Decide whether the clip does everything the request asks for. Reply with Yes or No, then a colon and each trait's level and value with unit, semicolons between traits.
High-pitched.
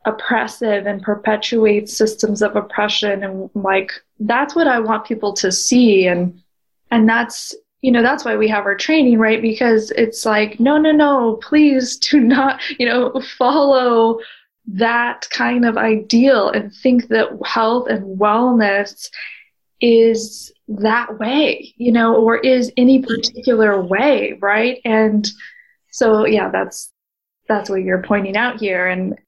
Yes: high, 225 Hz